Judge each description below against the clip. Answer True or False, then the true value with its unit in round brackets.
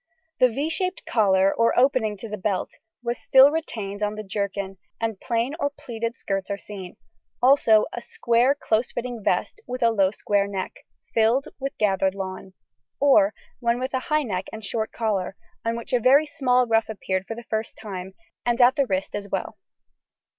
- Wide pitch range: False (4.0 semitones)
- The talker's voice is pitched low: False (225 Hz)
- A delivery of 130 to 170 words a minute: False (185 wpm)